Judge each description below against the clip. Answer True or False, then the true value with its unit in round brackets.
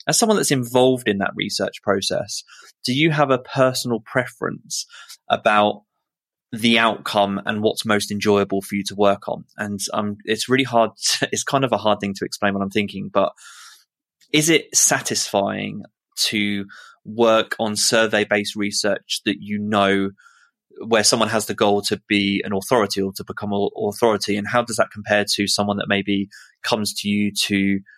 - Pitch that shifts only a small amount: True (2.1 semitones)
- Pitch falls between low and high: False (105 Hz)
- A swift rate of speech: False (180 wpm)